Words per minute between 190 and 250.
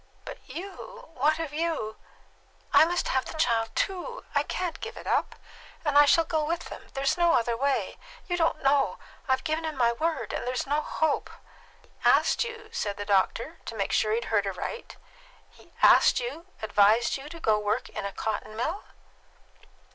Yes: average, 200 wpm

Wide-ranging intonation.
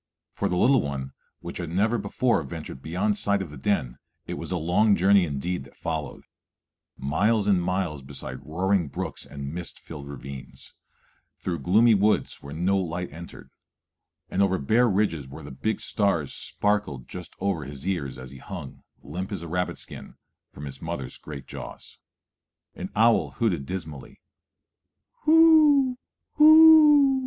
Yes: wide, 6.3 semitones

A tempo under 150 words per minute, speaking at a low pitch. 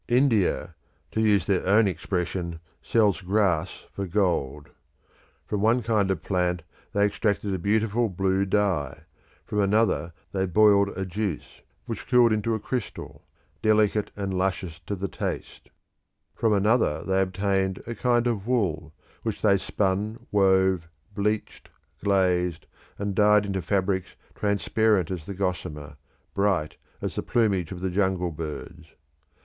Yes: average, 140 wpm; low, 100 Hz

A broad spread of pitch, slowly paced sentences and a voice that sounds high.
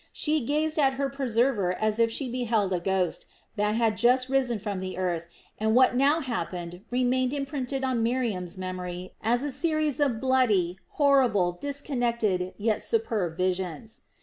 No: wide, 6.1 semitones; average, 155 wpm; high, 235 Hz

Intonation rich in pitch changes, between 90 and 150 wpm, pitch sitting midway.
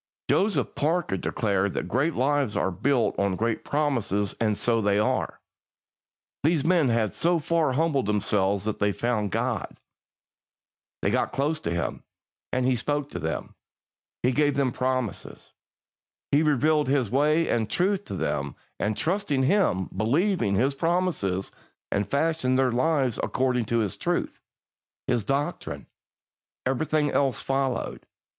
No: wide, 5.9 semitones; average, 140 wpm; low, 130 Hz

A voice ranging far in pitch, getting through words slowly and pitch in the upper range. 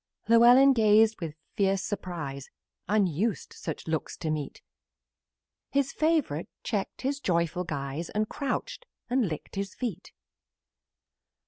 Yes: wide, 6.7 semitones; slow, 115 wpm; high, 195 Hz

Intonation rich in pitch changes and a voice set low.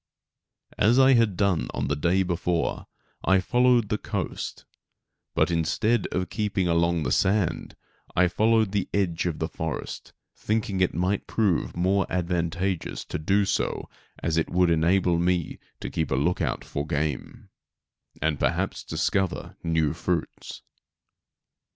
No: average, 3.2 semitones; very low, 90 Hz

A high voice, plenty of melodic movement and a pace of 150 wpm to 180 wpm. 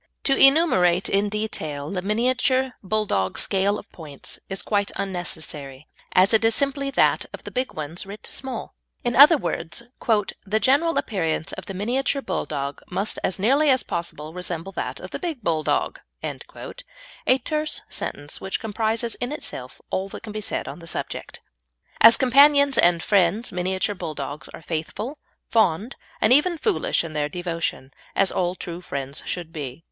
Yes: high, 200 Hz; wide, 7.4 semitones; average, 160 wpm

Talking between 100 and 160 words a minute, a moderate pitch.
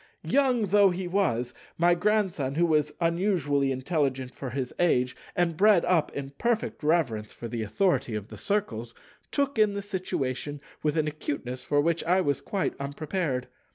Yes: average, 155 wpm; medium, 155 Hz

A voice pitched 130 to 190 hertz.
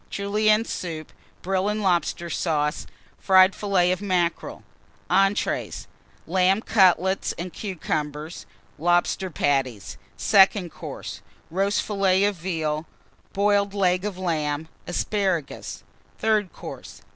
Yes: medium, 185 Hz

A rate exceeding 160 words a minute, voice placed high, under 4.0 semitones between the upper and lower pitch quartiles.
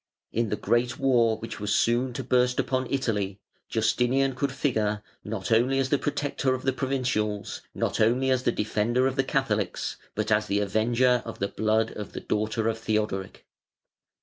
No: average, 175 wpm; low, 115 Hz; average, 3.4 semitones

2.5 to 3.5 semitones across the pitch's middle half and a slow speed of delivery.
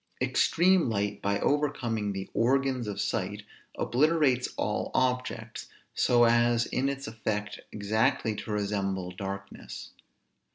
No: average, 4.0 semitones; slow, 115 wpm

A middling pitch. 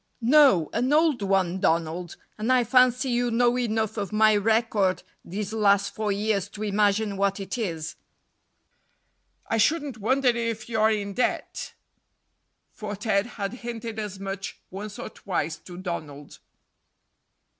No: high, 215 Hz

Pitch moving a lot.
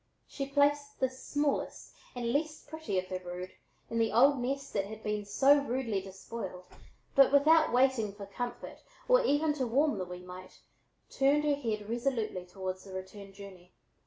Yes: wide, 6.4 semitones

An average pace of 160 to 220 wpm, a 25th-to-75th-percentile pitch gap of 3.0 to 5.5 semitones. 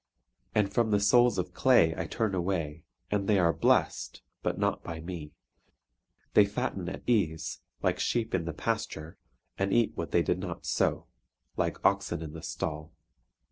Yes: average, 170 wpm; average, 4.2 semitones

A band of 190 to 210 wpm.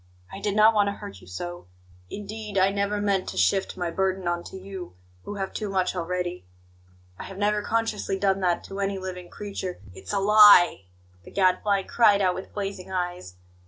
Yes: average, 195 wpm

